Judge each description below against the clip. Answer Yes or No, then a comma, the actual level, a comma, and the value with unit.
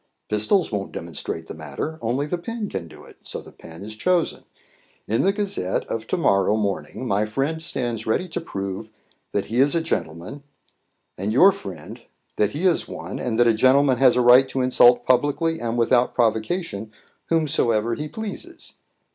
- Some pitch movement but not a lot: No, wide, 7.0 semitones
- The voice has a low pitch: Yes, low, 120 Hz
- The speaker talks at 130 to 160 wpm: No, average, 180 wpm